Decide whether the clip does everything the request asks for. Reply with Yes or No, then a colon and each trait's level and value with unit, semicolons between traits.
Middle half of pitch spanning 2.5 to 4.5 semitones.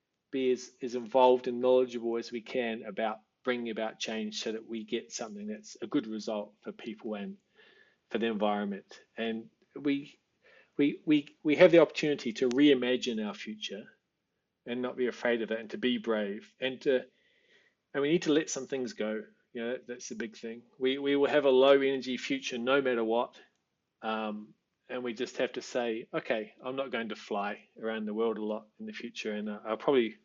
Yes: average, 3.4 semitones